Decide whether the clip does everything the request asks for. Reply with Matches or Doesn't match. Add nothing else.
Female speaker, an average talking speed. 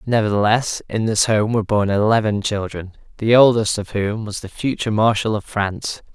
Doesn't match